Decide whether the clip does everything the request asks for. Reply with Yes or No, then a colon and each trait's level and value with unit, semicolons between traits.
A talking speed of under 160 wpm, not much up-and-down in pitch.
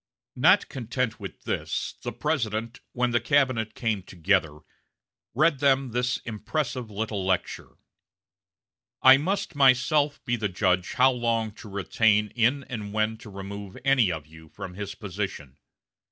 No: average, 140 wpm; average, 4.2 semitones